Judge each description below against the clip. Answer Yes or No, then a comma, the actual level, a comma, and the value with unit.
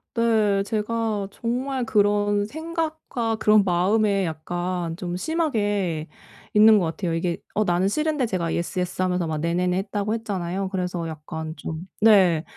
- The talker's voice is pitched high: Yes, high, 195 Hz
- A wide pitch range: No, average, 4.0 semitones